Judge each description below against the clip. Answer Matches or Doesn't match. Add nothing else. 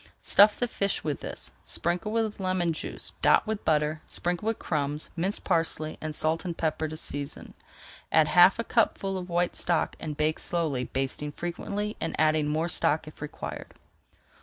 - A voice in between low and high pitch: Matches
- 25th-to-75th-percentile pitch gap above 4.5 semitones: Doesn't match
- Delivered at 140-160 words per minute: Doesn't match